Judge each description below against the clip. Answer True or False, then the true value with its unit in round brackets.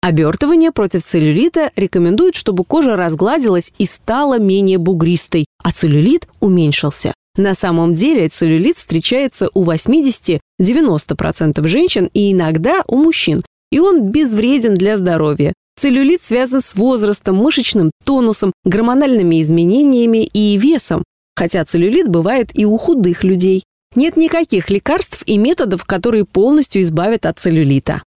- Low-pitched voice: False (200 Hz)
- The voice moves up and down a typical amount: False (7.3 semitones)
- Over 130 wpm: False (125 wpm)